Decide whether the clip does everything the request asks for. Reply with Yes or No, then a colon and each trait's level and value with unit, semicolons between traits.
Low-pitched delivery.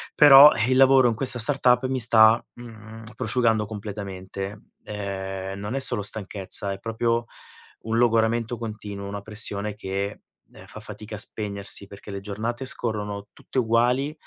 Yes: low, 110 Hz